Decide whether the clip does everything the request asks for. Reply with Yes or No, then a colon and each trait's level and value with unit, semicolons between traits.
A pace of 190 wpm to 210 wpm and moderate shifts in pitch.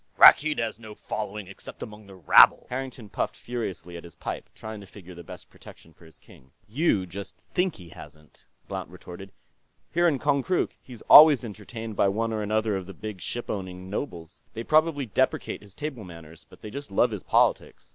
Yes: average, 195 wpm; average, 5.0 semitones